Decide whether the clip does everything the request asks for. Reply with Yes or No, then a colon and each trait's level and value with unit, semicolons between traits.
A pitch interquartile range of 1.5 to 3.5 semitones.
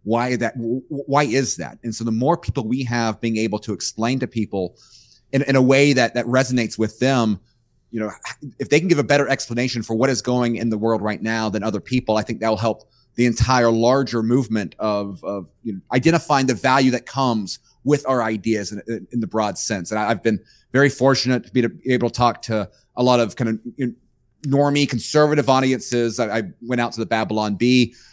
Yes: average, 2.8 semitones